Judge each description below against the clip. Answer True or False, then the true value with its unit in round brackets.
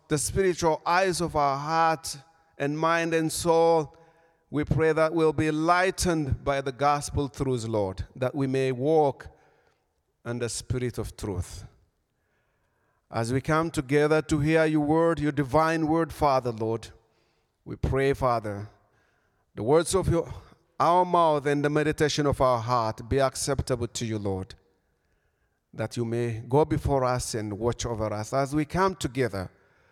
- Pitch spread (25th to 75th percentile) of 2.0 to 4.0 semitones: False (5.3 semitones)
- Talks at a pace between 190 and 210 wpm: False (155 wpm)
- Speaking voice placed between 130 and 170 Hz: True (140 Hz)